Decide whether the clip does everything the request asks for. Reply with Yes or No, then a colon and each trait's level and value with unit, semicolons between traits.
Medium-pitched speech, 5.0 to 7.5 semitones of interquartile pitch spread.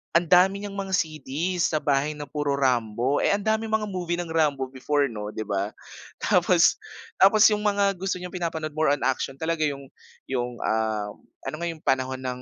Yes: medium, 150 Hz; wide, 5.4 semitones